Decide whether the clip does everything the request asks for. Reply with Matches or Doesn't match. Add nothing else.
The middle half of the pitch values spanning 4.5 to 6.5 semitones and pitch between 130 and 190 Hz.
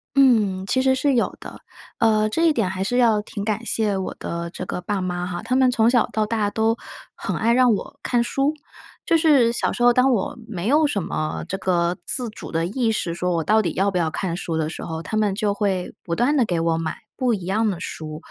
Doesn't match